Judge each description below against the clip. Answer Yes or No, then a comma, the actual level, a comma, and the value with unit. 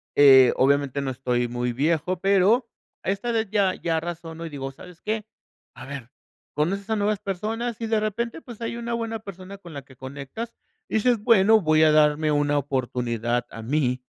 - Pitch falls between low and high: Yes, medium, 165 Hz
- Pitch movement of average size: No, wide, 7.5 semitones